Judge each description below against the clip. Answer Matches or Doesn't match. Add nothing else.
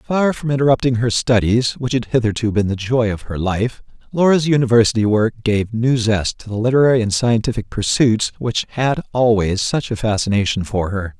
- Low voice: Matches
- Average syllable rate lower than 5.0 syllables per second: Doesn't match